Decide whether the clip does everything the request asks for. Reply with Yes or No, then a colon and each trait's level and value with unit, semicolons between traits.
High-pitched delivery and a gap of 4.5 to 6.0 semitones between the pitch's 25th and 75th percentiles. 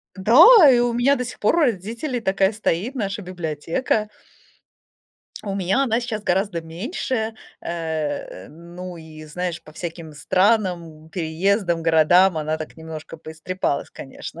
No: medium, 180 Hz; average, 5.2 semitones